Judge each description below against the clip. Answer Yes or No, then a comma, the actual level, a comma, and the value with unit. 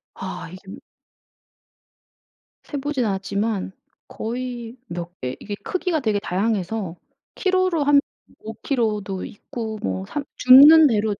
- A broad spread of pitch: Yes, wide, 6.2 semitones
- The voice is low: No, high, 220 Hz